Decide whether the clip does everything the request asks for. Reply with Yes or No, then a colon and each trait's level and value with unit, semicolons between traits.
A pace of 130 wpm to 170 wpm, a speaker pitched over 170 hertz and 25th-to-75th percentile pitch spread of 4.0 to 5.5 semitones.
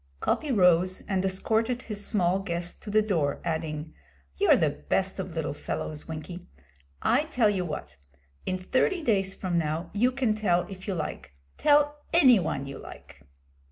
Yes: average, 165 wpm; high, 190 Hz; average, 4.7 semitones